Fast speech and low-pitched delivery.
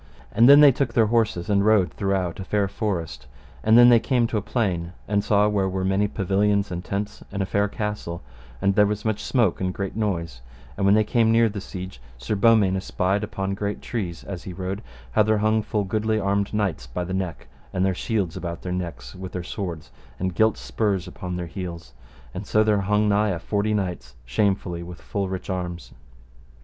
Yes: fast, 210 wpm; low, 100 Hz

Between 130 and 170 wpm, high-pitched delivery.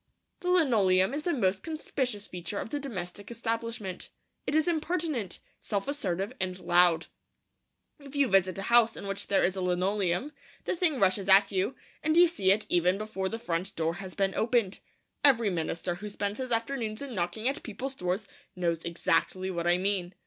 No: average, 185 wpm; high, 200 Hz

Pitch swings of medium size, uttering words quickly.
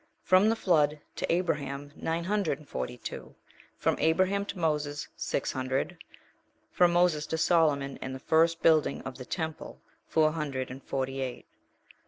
No: average, 3.8 semitones; average, 160 wpm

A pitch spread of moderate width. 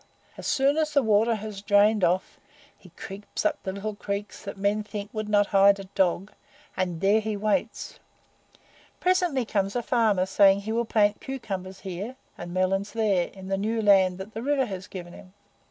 No: narrow, 2.3 semitones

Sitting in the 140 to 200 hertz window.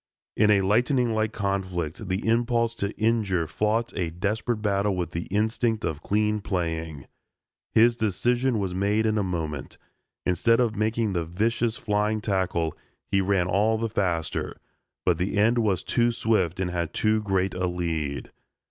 No: low, 105 Hz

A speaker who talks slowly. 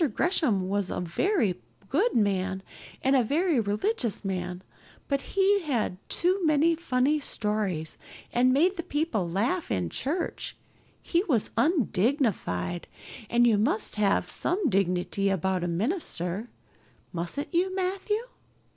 Yes: slow, 130 wpm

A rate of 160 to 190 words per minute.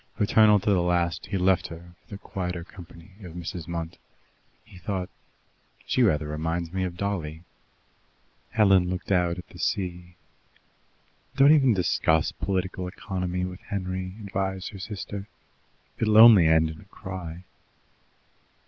No: average, 140 wpm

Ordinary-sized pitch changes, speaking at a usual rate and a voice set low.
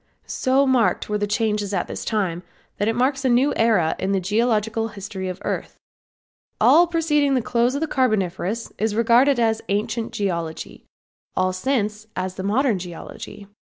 No: average, 4.3 semitones; average, 170 wpm; high, 220 Hz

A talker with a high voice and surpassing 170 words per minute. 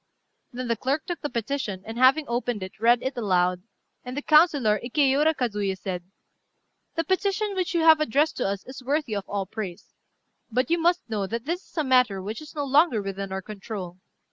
Yes: high, 245 Hz; average, 200 wpm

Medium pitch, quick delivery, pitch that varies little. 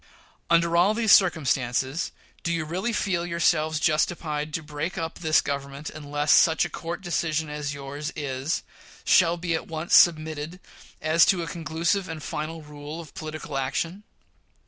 No: medium, 160 Hz; average, 155 wpm; narrow, 2.3 semitones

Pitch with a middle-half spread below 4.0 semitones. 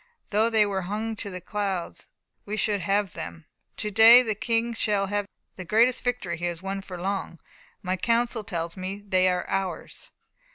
Yes: average, 3.1 semitones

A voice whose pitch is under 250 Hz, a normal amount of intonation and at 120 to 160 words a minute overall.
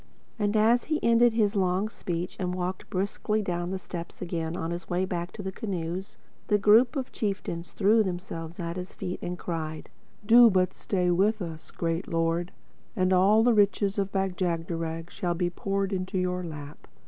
No: medium, 185 Hz; average, 3.0 semitones; average, 185 wpm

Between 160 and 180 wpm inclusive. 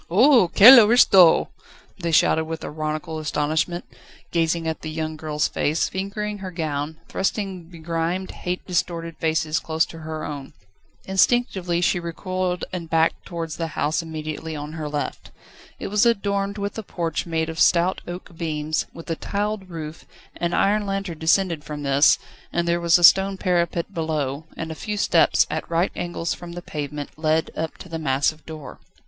Yes: average, 170 wpm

